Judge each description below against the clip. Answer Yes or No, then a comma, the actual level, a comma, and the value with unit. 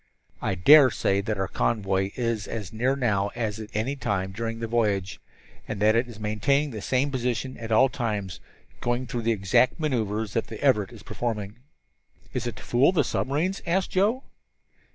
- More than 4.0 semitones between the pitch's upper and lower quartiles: No, average, 3.7 semitones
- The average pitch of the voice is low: Yes, low, 115 Hz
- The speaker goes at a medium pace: Yes, average, 190 wpm